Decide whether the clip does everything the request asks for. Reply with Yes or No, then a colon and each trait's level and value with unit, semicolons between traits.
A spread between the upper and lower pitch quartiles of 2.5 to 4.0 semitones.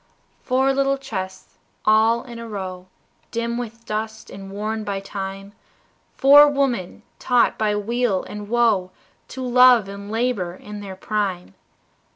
Yes: average, 3.6 semitones